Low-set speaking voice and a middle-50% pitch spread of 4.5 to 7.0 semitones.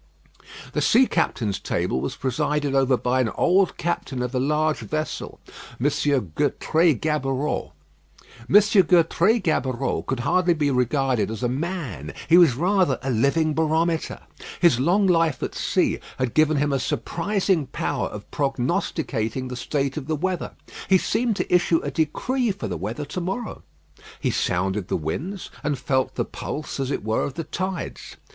No: medium, 150 Hz; average, 5.0 semitones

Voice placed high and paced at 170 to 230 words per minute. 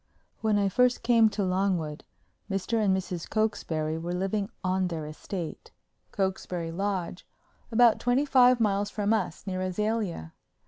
No: high, 195 Hz; average, 140 wpm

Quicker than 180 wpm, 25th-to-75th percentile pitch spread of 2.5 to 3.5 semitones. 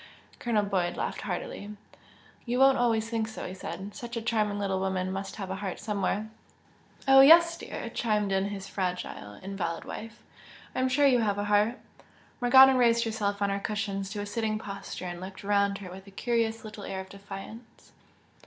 Yes: average, 190 wpm; average, 2.9 semitones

